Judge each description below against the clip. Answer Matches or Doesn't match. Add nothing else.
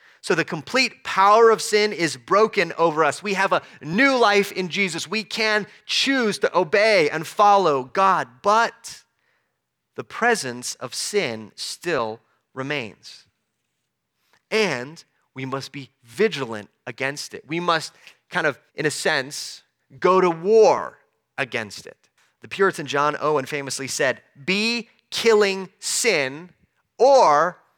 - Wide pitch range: Matches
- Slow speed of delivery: Matches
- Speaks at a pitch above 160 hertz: Matches